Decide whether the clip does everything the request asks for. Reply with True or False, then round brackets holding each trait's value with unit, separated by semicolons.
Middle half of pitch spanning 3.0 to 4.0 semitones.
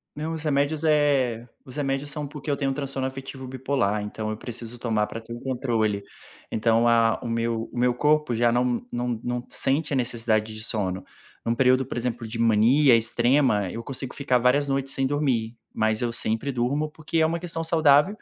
True (3.6 semitones)